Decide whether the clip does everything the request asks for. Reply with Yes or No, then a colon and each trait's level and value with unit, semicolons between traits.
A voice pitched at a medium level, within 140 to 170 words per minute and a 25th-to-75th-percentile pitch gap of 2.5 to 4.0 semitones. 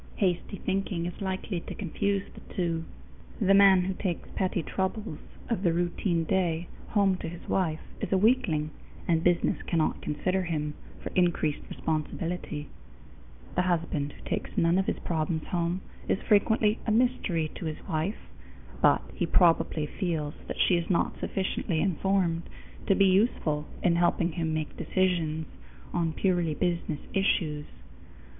Yes: medium, 175 Hz; average, 150 wpm; average, 2.9 semitones